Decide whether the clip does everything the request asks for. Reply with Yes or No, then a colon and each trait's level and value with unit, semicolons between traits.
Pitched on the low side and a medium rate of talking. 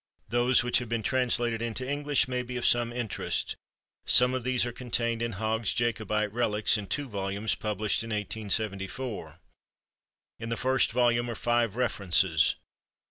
Yes: low, 115 Hz; average, 155 wpm